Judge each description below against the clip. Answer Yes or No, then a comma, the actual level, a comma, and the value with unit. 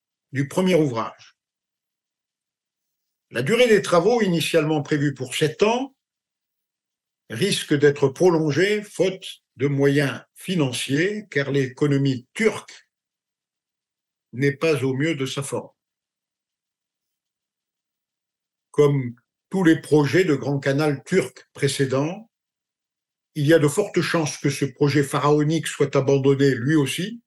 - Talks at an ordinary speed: No, slow, 115 wpm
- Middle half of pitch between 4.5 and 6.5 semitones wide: No, average, 4.0 semitones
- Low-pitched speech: No, medium, 150 Hz